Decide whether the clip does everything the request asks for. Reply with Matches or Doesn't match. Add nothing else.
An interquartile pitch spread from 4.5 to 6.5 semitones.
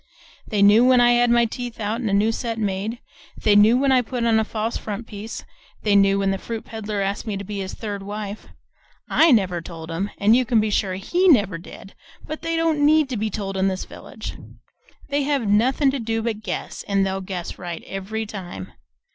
Doesn't match